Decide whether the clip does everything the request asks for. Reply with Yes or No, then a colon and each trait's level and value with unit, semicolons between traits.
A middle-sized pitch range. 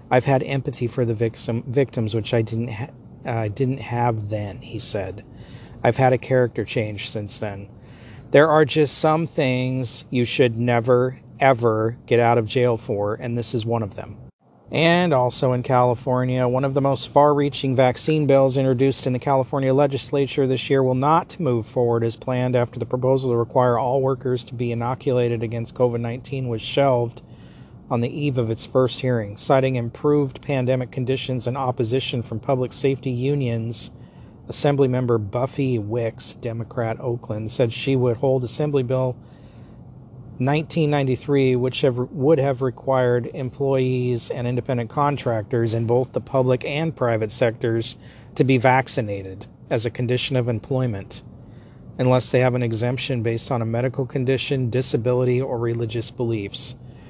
No: narrow, 2.2 semitones